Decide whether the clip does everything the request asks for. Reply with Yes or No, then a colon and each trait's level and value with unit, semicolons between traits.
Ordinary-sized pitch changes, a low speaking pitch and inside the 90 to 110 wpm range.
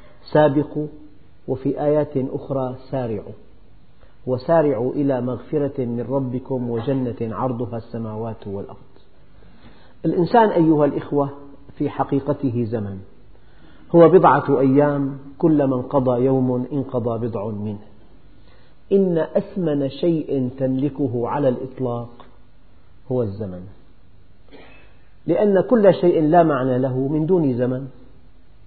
Yes: average, 3.6 semitones; low, 130 Hz; average, 100 wpm